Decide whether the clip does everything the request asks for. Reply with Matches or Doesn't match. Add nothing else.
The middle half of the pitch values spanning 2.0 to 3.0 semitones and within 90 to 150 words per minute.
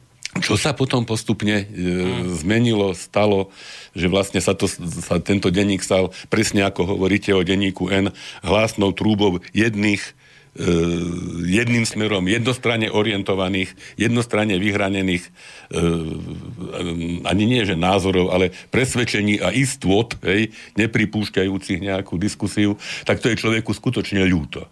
Matches